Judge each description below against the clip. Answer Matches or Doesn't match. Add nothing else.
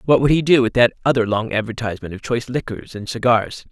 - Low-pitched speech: Matches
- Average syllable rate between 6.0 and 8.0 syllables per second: Matches